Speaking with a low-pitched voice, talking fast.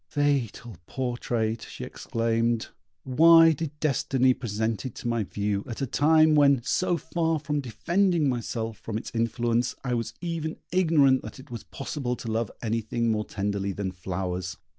No: low, 120 Hz; average, 160 wpm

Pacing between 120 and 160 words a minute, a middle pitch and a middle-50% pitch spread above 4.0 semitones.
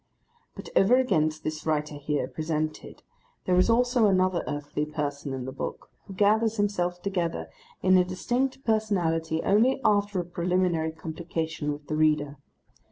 Yes: average, 150 wpm; medium, 175 Hz; average, 4.7 semitones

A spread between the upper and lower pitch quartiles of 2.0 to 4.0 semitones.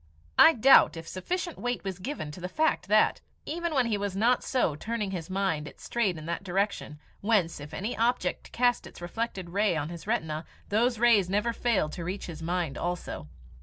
No: wide, 5.4 semitones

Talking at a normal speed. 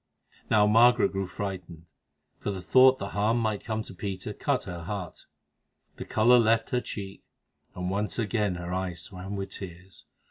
Yes: average, 170 wpm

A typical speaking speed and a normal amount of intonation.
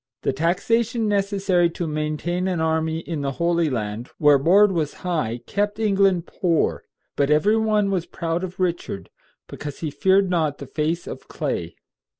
Yes: average, 160 wpm; average, 4.2 semitones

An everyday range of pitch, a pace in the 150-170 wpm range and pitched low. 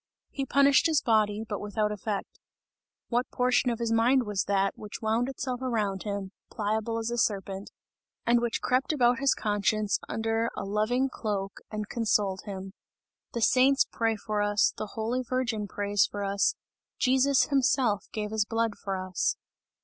No: average, 3.2 semitones; average, 165 wpm; high, 220 Hz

